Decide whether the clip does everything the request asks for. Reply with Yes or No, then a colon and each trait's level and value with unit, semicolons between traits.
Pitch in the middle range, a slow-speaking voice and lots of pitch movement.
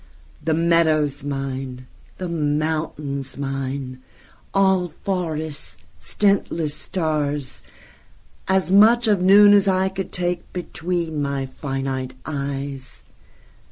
No: medium, 155 Hz; slow, 85 wpm; average, 4.7 semitones